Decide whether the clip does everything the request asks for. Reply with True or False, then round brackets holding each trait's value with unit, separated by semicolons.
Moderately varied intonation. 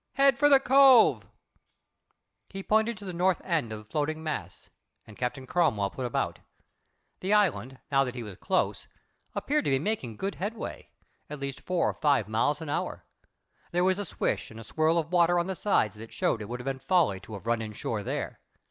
False (8.3 semitones)